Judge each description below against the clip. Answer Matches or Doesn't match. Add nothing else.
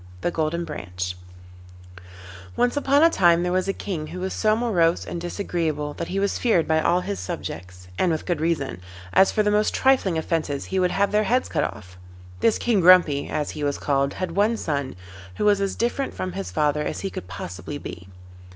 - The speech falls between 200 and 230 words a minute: Matches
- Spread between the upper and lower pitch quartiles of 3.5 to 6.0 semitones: Matches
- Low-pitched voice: Doesn't match